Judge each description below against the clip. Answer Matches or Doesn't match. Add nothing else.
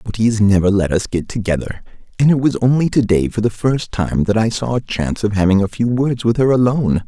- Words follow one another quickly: Matches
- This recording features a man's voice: Matches